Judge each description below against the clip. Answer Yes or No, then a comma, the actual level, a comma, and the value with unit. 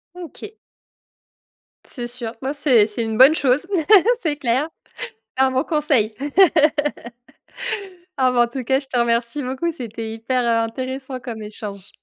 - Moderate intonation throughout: Yes, average, 3.1 semitones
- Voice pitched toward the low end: No, very high, 250 Hz